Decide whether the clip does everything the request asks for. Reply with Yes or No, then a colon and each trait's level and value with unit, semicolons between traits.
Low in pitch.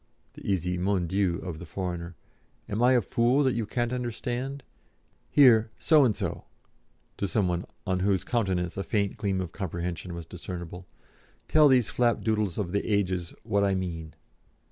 Yes: low, 100 Hz